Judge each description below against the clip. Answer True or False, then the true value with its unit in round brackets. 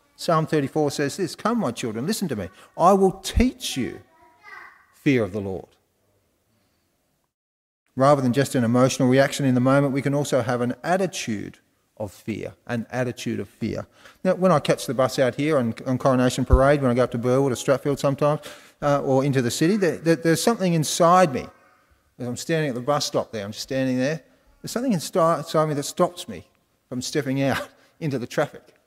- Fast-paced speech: False (195 wpm)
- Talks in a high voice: False (140 Hz)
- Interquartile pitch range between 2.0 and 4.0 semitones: False (4.7 semitones)